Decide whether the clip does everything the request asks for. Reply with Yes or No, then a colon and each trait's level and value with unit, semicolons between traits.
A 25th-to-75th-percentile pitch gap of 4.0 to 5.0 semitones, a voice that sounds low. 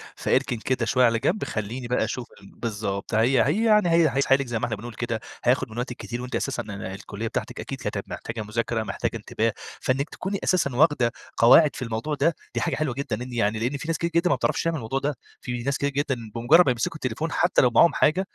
Yes: average, 4.4 semitones; low, 125 Hz